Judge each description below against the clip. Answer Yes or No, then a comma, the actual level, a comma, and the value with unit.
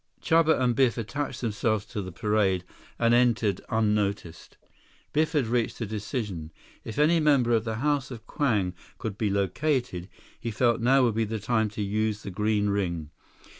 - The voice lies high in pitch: No, low, 110 Hz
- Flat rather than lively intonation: No, average, 3.3 semitones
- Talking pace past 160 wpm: Yes, average, 170 wpm